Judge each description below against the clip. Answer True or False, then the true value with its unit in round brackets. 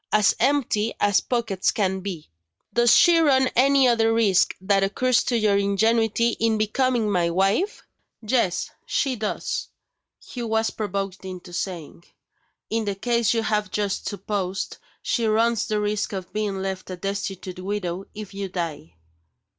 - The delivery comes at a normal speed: True (150 wpm)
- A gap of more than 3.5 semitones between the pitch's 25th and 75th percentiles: False (3.0 semitones)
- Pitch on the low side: False (210 Hz)